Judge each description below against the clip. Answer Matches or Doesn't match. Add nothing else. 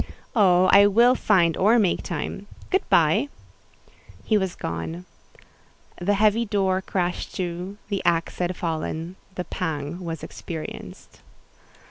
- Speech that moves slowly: Matches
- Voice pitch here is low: Doesn't match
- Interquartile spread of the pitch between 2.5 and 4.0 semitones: Matches